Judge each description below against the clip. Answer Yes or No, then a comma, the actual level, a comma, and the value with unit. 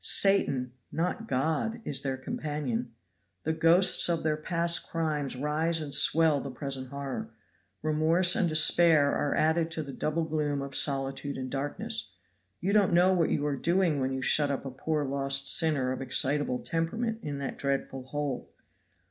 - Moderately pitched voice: Yes, medium, 150 Hz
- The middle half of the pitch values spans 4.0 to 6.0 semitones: No, average, 3.2 semitones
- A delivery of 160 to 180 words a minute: Yes, average, 165 wpm